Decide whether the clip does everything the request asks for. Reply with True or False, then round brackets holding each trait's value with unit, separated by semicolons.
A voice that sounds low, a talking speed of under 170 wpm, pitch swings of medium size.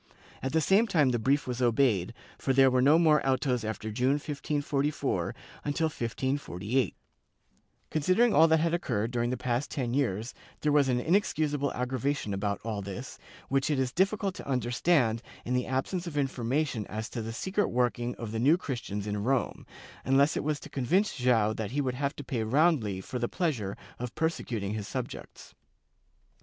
False (130 Hz; 180 wpm; 4.3 semitones)